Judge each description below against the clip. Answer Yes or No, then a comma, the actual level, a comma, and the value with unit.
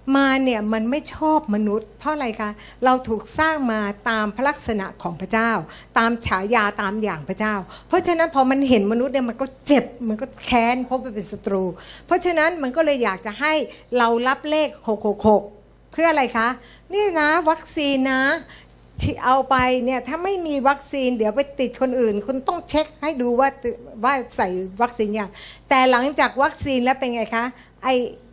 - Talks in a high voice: Yes, very high, 255 Hz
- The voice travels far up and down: No, average, 4.3 semitones